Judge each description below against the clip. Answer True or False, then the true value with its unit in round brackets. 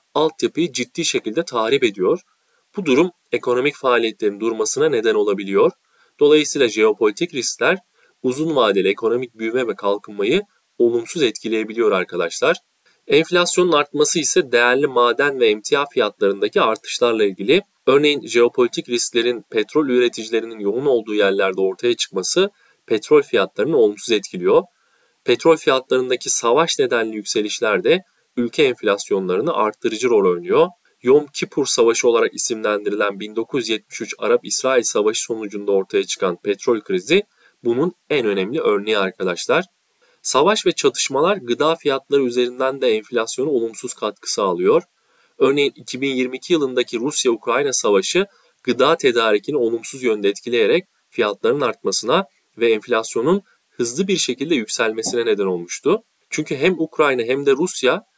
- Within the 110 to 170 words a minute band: True (120 wpm)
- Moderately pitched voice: True (175 Hz)